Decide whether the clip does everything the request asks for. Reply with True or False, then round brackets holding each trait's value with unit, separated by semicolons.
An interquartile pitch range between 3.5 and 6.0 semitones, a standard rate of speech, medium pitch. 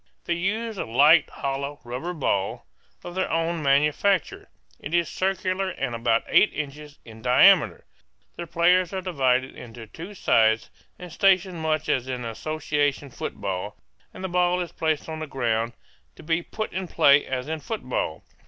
True (5.6 semitones; 160 wpm; 155 Hz)